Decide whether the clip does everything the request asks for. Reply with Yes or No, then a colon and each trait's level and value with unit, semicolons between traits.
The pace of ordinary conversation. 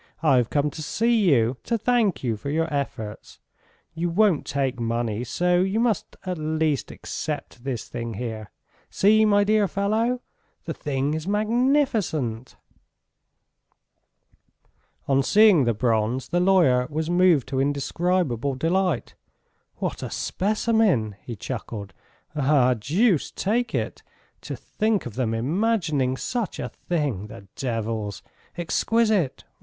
No: slow, 130 wpm